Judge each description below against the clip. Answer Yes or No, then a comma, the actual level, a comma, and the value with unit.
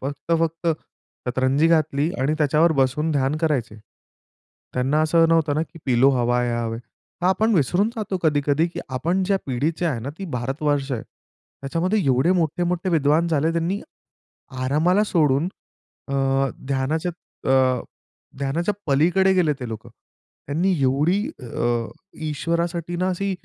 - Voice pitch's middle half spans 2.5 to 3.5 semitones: No, average, 4.1 semitones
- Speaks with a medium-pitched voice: Yes, medium, 155 Hz